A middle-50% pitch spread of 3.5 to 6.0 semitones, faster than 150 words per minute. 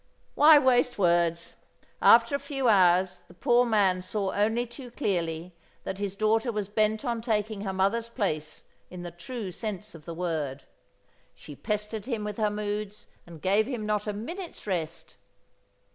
Yes: average, 4.2 semitones; average, 165 wpm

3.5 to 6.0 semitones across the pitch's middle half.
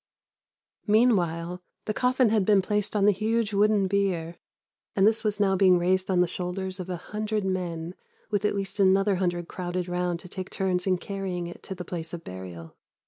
No: narrow, 2.6 semitones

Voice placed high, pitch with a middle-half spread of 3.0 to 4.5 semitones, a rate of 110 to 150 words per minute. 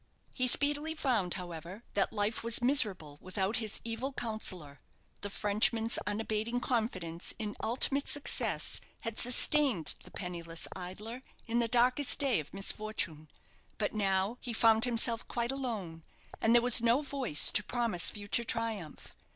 Yes: high, 225 Hz; average, 4.1 semitones; average, 145 wpm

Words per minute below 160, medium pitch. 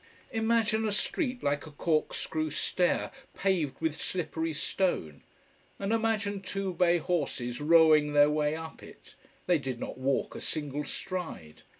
Yes: average, 140 wpm; medium, 160 Hz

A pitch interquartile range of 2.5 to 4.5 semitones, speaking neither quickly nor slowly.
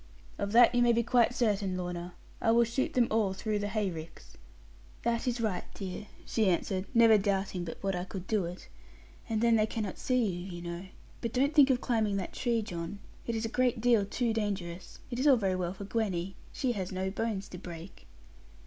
No: average, 3.9 semitones; fast, 215 wpm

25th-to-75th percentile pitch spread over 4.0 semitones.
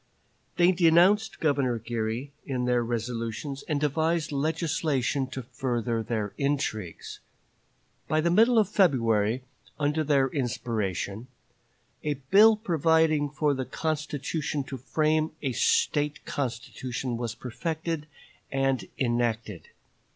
Yes: average, 4.6 semitones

